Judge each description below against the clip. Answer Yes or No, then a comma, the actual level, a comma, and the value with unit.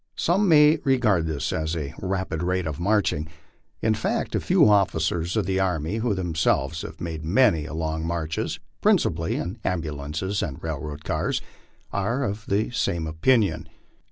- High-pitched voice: No, very low, 85 Hz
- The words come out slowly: No, average, 155 wpm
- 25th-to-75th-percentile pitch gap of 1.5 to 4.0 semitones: No, average, 4.7 semitones